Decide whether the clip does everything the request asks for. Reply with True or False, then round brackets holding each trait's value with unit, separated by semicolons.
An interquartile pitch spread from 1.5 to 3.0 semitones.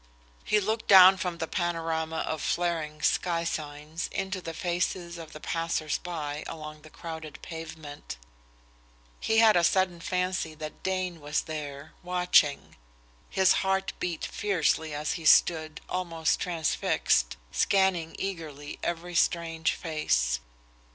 True (2.6 semitones)